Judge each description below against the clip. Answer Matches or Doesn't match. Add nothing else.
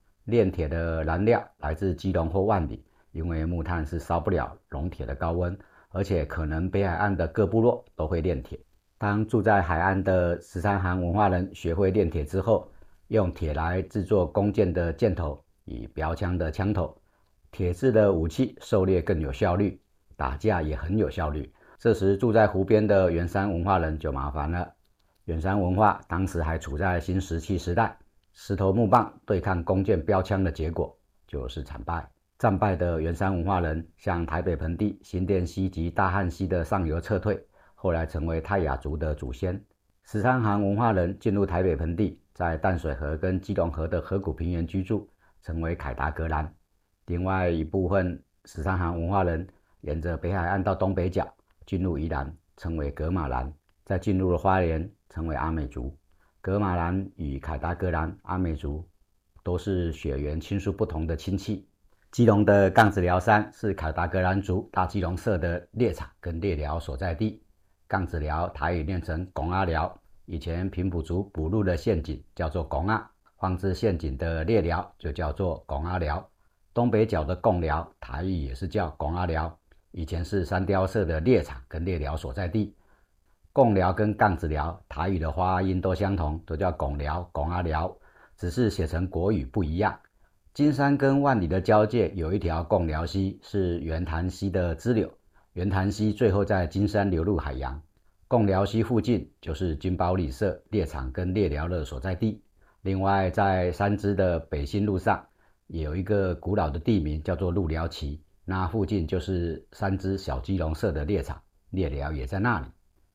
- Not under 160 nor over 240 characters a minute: Doesn't match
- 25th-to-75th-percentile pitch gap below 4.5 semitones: Matches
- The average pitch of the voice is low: Matches